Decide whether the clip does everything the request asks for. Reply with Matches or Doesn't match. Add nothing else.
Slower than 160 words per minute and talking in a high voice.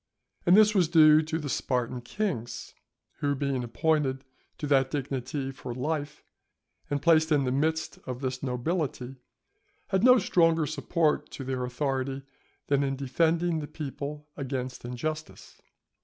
Doesn't match